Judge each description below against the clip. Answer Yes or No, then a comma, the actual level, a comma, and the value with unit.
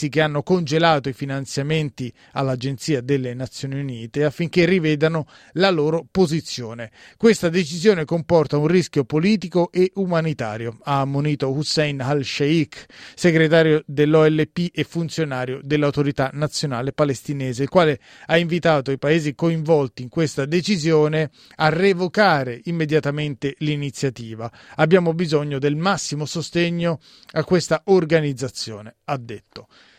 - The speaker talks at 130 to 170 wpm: No, slow, 115 wpm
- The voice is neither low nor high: Yes, medium, 150 Hz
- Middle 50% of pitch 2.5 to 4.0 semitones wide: Yes, average, 3.3 semitones